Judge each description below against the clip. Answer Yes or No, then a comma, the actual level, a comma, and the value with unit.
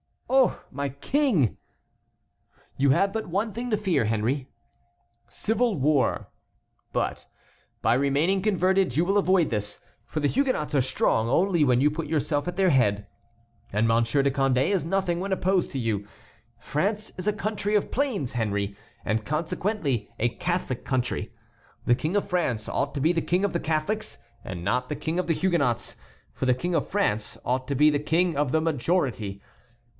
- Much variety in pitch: Yes, wide, 7.1 semitones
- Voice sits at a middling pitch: Yes, medium, 150 Hz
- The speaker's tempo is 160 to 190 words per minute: Yes, average, 175 wpm